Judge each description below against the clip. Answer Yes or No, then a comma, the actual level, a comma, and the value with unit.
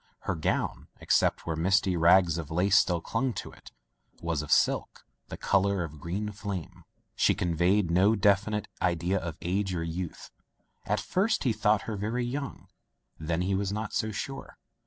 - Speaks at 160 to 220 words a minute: Yes, average, 170 wpm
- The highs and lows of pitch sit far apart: No, average, 3.6 semitones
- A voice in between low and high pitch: No, very low, 95 Hz